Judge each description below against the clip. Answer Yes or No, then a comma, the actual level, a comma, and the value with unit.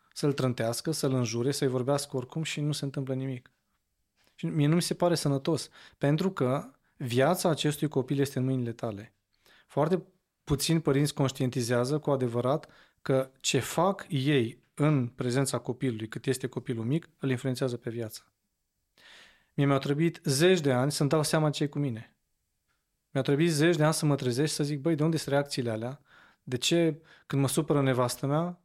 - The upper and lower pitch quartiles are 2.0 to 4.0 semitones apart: Yes, average, 3.1 semitones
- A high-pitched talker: No, medium, 140 Hz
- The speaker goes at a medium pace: No, fast, 175 wpm